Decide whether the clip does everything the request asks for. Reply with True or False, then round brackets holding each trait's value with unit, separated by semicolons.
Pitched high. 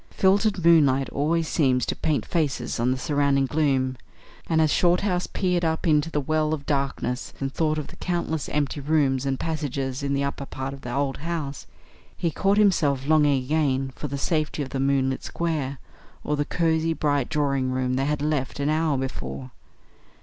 False (145 Hz)